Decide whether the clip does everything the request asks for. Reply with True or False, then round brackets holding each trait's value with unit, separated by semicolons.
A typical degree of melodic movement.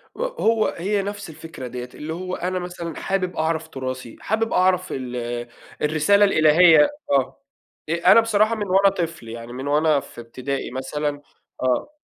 False (6.1 semitones)